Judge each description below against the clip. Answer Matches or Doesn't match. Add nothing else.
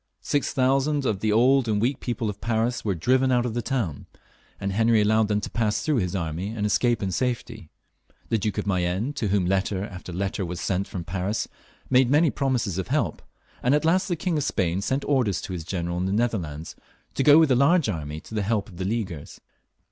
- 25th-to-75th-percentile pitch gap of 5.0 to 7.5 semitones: Matches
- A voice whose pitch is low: Matches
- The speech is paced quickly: Matches